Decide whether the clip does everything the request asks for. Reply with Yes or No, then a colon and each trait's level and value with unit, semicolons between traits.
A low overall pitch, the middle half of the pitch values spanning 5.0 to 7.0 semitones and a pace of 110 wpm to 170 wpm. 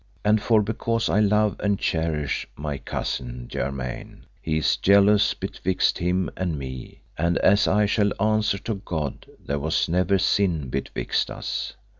Yes: very low, 90 Hz; wide, 5.5 semitones; average, 150 wpm